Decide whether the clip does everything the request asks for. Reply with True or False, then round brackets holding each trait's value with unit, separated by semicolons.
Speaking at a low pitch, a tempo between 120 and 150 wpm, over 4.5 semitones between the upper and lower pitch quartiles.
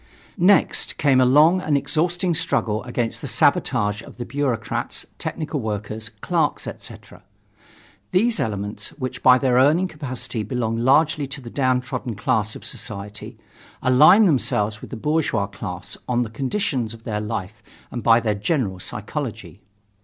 True (125 Hz; 145 wpm; 5.0 semitones)